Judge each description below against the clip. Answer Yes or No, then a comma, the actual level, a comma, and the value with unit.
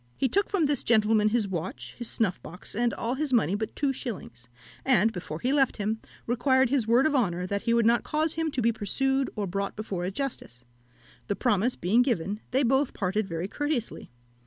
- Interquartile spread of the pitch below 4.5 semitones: No, average, 5.0 semitones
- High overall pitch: Yes, high, 230 Hz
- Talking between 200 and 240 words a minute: Yes, fast, 205 wpm